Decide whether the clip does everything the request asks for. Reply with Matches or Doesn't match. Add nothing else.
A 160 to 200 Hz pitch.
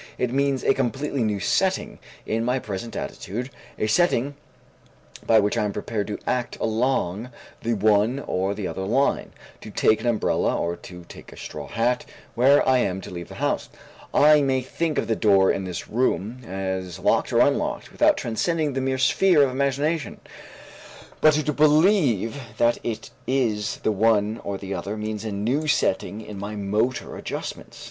Doesn't match